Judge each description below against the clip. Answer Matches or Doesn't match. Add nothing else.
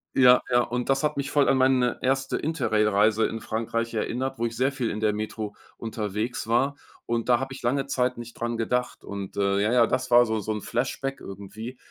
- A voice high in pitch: Doesn't match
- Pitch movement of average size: Matches